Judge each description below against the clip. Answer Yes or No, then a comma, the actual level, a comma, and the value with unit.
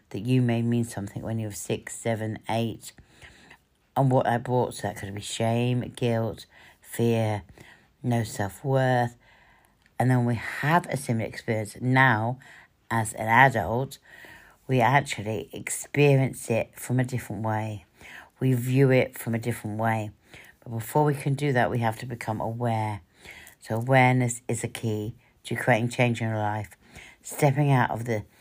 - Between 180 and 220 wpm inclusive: No, average, 165 wpm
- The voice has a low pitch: Yes, low, 115 Hz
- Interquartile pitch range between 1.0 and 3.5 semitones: Yes, narrow, 2.5 semitones